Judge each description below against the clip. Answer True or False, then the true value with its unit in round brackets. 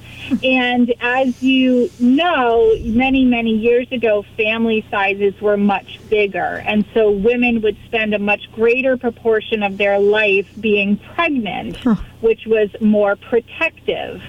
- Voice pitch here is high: True (225 Hz)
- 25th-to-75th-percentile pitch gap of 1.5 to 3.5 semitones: True (2.8 semitones)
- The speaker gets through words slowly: True (130 wpm)